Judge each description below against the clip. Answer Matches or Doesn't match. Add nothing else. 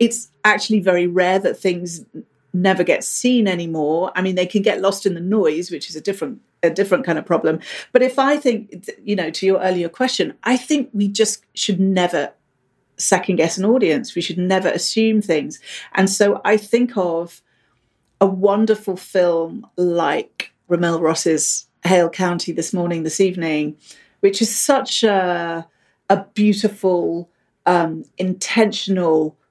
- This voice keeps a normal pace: Matches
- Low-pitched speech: Doesn't match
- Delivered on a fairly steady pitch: Doesn't match